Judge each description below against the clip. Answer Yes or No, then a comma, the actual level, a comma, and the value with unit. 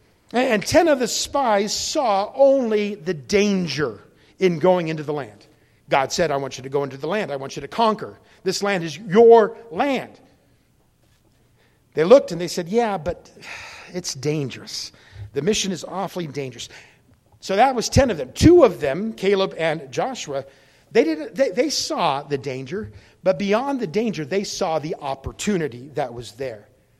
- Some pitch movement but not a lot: No, wide, 7.2 semitones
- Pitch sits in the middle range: Yes, medium, 180 Hz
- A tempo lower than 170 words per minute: No, average, 175 wpm